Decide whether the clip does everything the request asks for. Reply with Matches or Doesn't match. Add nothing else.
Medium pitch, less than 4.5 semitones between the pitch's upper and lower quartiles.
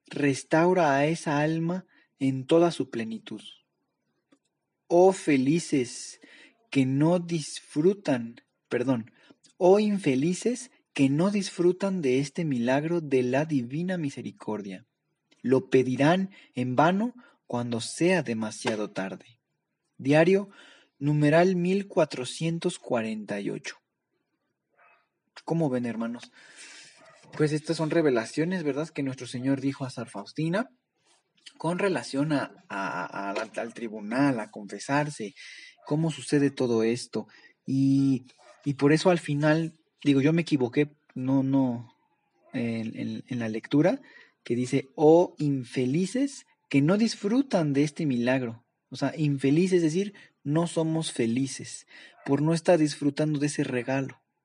Doesn't match